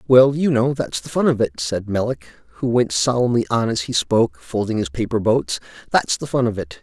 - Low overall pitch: Yes, low, 120 Hz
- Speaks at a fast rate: Yes, fast, 230 wpm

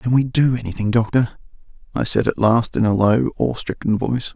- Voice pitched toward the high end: No, low, 115 Hz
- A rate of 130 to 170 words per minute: No, fast, 205 wpm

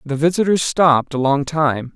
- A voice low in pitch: No, medium, 150 Hz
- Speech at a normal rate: Yes, average, 185 wpm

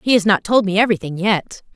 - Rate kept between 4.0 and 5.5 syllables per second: No, 6.4 syllables/s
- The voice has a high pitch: Yes, high, 200 Hz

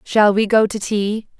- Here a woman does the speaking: Yes, female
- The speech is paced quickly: Yes, fast, 215 wpm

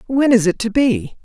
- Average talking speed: No, fast, 240 wpm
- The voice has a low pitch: No, high, 240 Hz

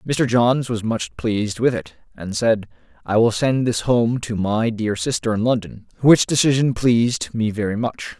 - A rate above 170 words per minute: Yes, average, 190 wpm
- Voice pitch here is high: No, low, 115 Hz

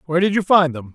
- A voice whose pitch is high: No, medium, 165 Hz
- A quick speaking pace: Yes, fast, 315 wpm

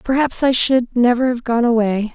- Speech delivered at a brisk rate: No, average, 195 wpm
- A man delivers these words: No, female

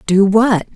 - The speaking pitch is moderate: No, high, 205 Hz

